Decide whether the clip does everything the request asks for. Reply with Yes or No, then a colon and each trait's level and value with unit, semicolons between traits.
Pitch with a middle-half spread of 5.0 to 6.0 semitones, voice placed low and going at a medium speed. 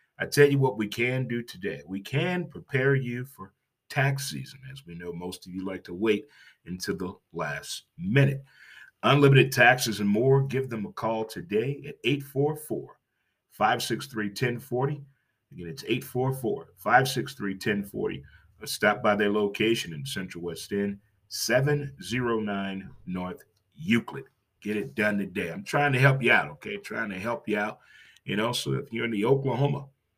Yes: average, 5.3 semitones; low, 115 Hz; average, 160 wpm